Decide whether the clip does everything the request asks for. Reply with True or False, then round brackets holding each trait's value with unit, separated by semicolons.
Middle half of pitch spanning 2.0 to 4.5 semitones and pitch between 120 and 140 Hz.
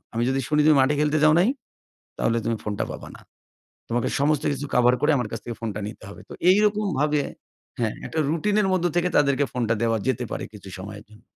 False (5.1 semitones; 135 Hz)